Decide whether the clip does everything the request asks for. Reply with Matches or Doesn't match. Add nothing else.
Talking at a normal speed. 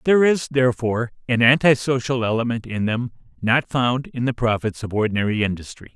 Matches